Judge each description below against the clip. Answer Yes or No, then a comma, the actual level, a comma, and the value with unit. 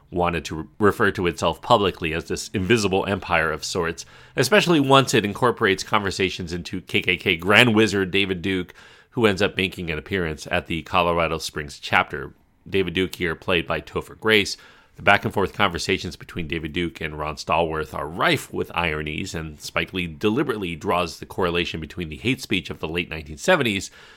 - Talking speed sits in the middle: Yes, average, 180 wpm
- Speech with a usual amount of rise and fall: Yes, average, 3.5 semitones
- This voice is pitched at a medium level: No, very low, 90 Hz